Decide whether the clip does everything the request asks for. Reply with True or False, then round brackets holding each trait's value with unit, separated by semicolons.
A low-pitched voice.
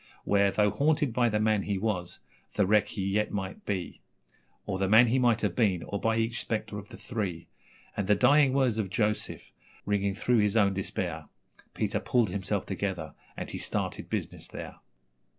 True (105 Hz)